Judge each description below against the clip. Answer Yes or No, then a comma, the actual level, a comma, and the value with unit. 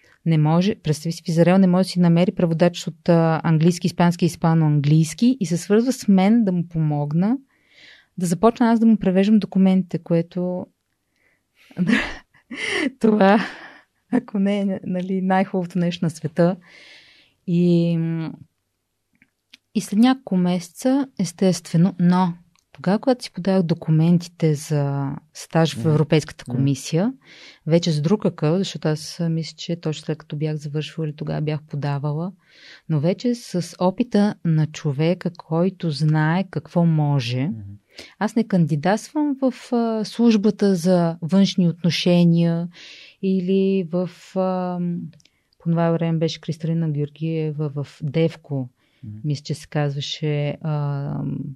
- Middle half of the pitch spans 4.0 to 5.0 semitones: No, average, 3.5 semitones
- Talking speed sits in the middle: Yes, average, 125 wpm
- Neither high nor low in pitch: Yes, medium, 170 Hz